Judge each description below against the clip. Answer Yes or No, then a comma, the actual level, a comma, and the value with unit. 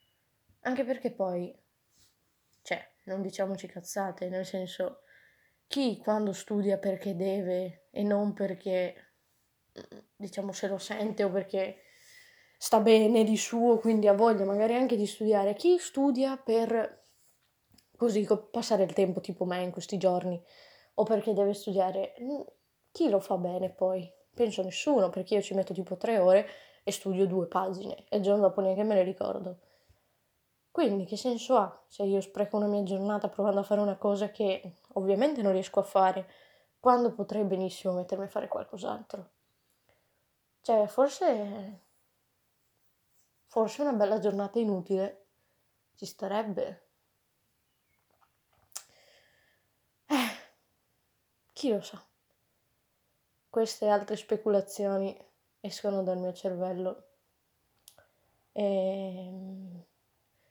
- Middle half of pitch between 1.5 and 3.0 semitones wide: Yes, narrow, 2.6 semitones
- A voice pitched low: No, high, 200 Hz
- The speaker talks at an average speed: Yes, average, 125 wpm